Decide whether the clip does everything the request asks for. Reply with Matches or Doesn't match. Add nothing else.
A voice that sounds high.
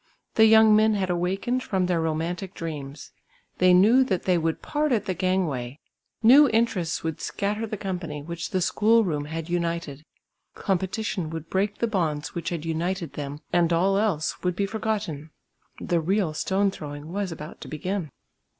Doesn't match